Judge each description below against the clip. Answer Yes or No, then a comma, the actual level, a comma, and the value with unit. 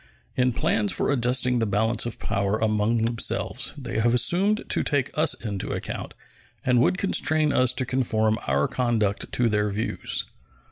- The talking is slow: No, average, 160 wpm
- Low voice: Yes, low, 115 Hz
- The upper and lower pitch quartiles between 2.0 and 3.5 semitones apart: Yes, average, 3.0 semitones